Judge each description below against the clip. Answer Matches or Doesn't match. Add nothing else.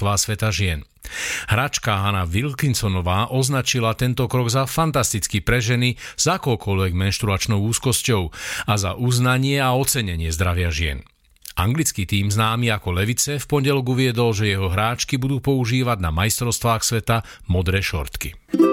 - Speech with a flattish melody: Doesn't match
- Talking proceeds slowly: Doesn't match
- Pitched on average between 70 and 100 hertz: Doesn't match